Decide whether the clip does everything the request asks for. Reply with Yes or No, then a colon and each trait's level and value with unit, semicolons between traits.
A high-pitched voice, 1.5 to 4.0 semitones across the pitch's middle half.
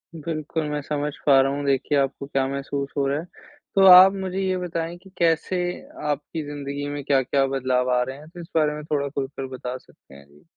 No: medium, 145 Hz; average, 3.1 semitones